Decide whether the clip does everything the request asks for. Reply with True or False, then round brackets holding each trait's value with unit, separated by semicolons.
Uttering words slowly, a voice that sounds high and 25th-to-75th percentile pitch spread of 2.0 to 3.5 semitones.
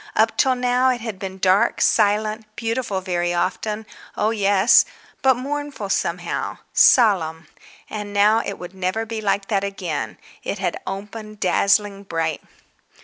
True (130 wpm; 205 Hz; 3.0 semitones)